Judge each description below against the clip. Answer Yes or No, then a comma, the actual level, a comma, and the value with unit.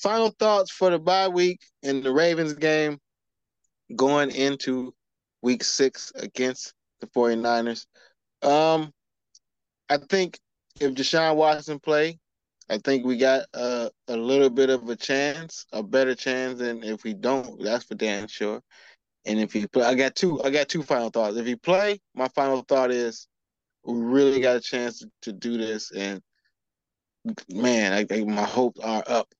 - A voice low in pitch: Yes, low, 130 Hz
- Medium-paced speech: Yes, average, 165 wpm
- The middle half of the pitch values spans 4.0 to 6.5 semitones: Yes, average, 4.4 semitones